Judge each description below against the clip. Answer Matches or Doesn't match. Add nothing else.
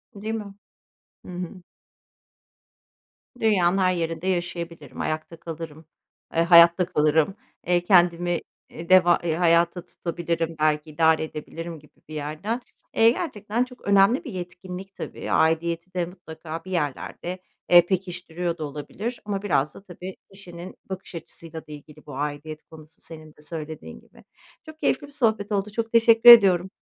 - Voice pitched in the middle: Matches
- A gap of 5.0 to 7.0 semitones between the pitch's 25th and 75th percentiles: Doesn't match